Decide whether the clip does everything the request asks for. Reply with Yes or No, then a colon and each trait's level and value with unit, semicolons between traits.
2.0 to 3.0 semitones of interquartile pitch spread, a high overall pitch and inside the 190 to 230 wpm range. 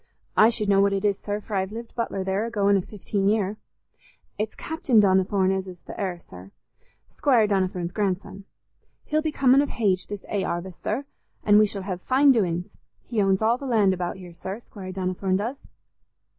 Yes: average, 2.7 semitones; high, 200 Hz; average, 195 wpm